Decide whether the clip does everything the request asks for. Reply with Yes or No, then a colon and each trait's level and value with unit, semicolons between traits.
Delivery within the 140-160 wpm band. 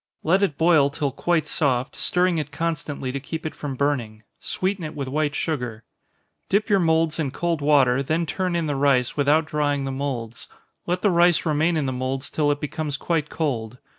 No: average, 195 wpm